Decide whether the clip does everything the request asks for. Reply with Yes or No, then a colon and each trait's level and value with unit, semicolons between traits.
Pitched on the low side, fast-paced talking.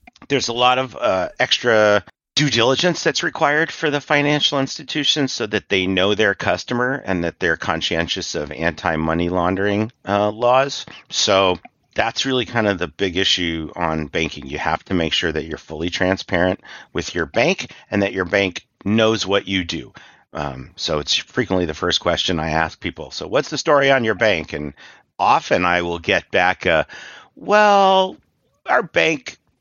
Yes: low, 100 Hz; fast, 175 wpm